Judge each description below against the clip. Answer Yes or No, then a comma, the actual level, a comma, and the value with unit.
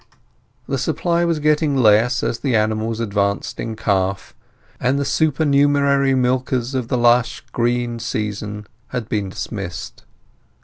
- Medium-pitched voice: No, low, 120 Hz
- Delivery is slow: Yes, slow, 130 wpm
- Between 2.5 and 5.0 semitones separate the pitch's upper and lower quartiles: Yes, average, 4.3 semitones